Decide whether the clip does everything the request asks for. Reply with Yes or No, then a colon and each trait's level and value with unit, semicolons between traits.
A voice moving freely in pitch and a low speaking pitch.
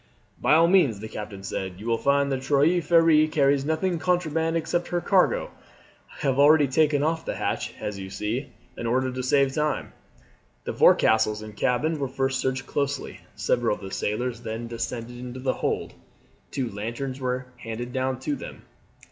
No: average, 4.6 semitones; low, 130 Hz